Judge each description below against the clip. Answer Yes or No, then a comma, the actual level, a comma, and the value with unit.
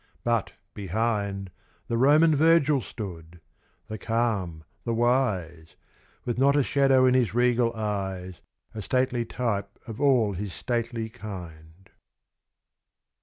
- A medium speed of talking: No, slow, 120 wpm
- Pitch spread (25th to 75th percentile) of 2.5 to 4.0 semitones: No, average, 4.6 semitones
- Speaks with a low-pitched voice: Yes, low, 115 Hz